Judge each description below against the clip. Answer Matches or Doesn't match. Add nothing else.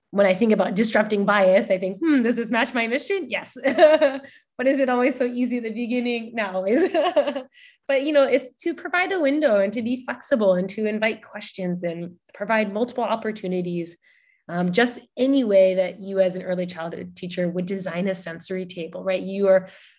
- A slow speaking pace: Doesn't match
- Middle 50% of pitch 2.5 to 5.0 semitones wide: Doesn't match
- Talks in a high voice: Matches